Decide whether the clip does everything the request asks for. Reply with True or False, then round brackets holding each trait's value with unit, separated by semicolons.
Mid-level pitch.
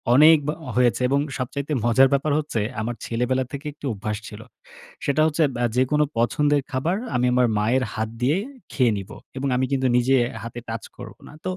False (130 Hz)